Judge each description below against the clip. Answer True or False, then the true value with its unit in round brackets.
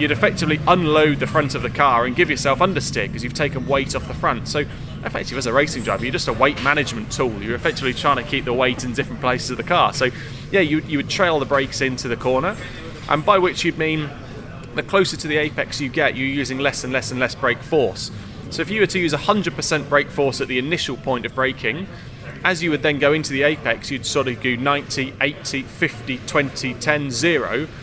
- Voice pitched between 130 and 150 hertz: True (140 Hz)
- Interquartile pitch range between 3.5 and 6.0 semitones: False (3.1 semitones)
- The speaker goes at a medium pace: False (235 wpm)